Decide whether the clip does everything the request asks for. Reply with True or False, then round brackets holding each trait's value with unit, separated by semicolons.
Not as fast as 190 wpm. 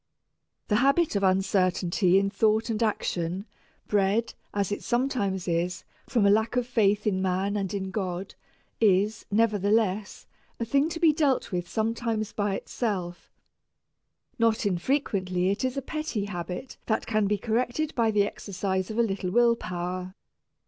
True (155 wpm)